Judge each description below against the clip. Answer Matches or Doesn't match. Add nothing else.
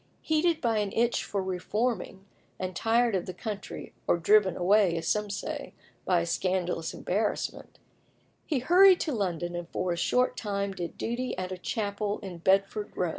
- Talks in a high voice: Matches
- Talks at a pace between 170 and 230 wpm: Matches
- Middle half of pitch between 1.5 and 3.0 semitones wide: Doesn't match